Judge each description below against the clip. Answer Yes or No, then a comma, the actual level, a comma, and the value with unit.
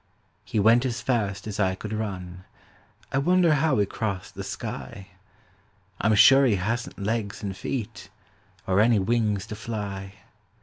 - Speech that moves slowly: No, average, 150 wpm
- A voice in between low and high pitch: No, low, 105 Hz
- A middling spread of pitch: Yes, average, 3.1 semitones